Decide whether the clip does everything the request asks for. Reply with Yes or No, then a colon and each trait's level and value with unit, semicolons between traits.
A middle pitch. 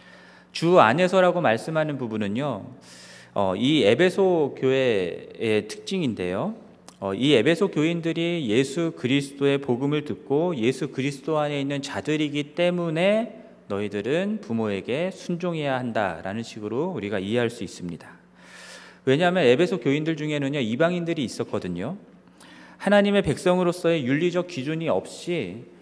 Yes: medium, 145 Hz